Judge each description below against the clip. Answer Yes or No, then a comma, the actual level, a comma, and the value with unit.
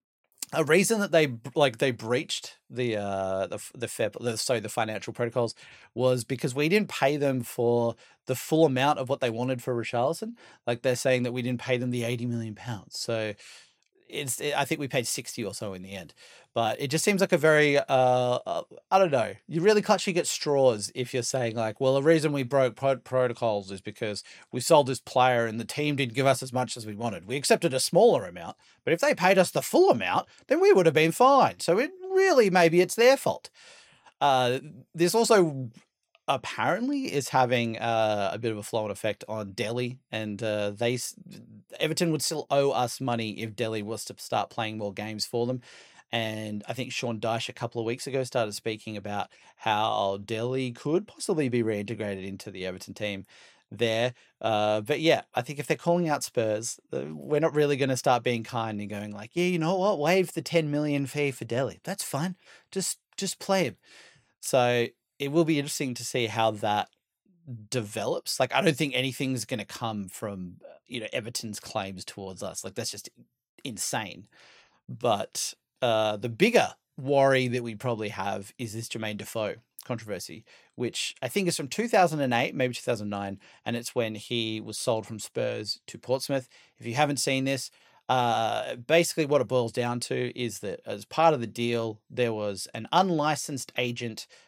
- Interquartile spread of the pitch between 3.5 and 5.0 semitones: Yes, average, 4.7 semitones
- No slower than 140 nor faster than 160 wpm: No, average, 195 wpm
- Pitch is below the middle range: Yes, low, 125 Hz